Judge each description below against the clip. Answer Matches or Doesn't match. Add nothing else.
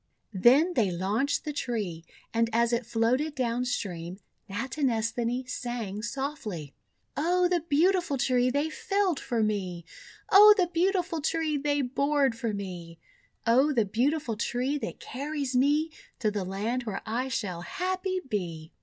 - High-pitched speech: Matches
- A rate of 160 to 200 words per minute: Doesn't match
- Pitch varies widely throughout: Matches